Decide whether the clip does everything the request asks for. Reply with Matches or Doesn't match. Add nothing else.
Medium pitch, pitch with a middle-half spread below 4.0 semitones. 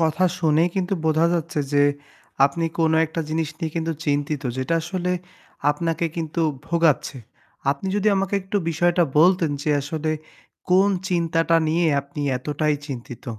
Matches